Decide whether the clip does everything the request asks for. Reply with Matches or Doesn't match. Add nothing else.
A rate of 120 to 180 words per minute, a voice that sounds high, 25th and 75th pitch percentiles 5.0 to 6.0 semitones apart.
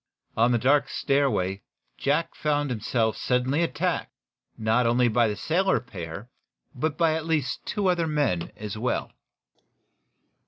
Doesn't match